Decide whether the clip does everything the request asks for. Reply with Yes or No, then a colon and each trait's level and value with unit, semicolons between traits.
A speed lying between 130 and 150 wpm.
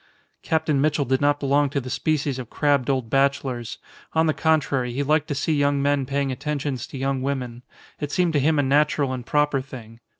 No: fast, 205 wpm